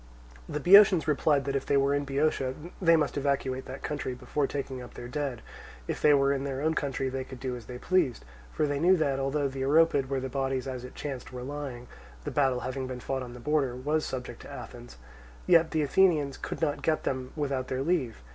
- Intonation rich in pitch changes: No, narrow, 2.4 semitones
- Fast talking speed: Yes, fast, 225 wpm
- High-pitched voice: No, low, 135 Hz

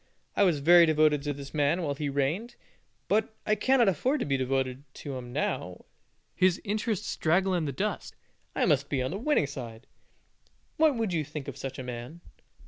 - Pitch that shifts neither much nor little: No, wide, 6.1 semitones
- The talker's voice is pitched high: No, medium, 150 Hz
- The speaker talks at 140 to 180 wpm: No, average, 195 wpm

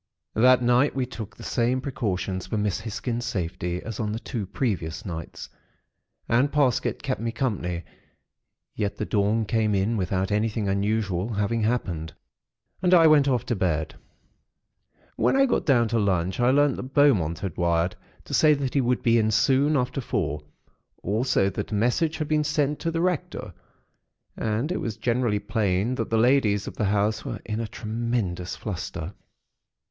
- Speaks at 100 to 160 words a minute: No, average, 175 wpm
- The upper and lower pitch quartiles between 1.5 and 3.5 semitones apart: No, average, 4.5 semitones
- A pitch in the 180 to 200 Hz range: No, low, 110 Hz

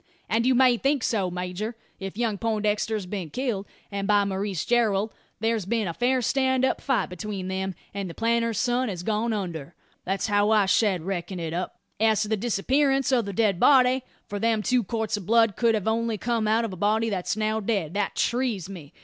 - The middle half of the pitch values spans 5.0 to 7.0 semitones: No, average, 3.2 semitones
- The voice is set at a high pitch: Yes, high, 215 Hz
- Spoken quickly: Yes, fast, 210 wpm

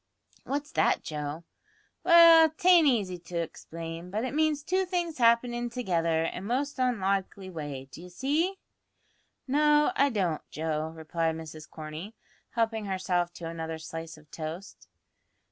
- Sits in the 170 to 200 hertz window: Yes, high, 190 Hz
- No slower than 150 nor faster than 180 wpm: No, average, 140 wpm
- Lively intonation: Yes, wide, 8.7 semitones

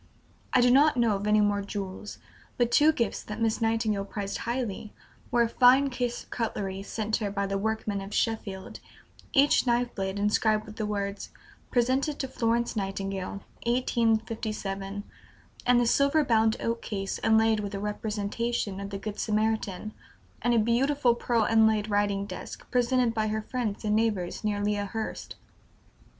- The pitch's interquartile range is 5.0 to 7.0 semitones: No, average, 2.7 semitones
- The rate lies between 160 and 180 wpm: Yes, average, 165 wpm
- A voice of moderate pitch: No, high, 220 Hz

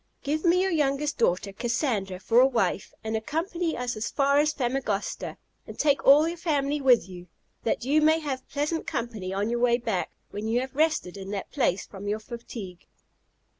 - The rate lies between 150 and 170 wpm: No, average, 190 wpm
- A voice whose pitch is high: Yes, high, 245 Hz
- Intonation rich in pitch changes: Yes, wide, 5.7 semitones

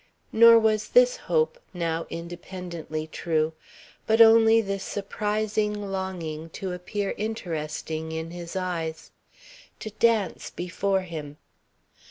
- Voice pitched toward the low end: No, high, 190 Hz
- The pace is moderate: No, slow, 110 wpm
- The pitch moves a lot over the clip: No, average, 4.7 semitones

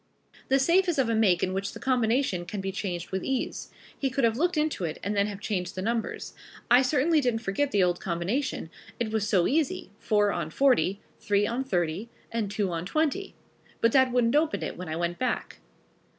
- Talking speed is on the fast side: Yes, fast, 210 wpm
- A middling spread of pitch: No, wide, 5.9 semitones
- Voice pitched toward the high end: Yes, high, 220 Hz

